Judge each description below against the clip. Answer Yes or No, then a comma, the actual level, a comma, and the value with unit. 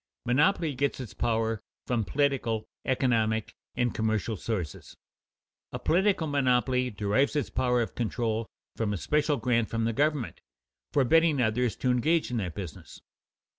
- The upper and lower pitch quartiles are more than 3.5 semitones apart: Yes, average, 4.1 semitones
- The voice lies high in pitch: No, low, 125 Hz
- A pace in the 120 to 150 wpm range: Yes, average, 140 wpm